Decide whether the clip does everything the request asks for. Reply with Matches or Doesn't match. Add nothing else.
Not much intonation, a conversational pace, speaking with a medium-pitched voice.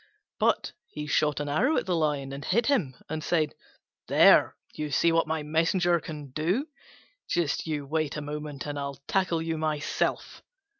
Matches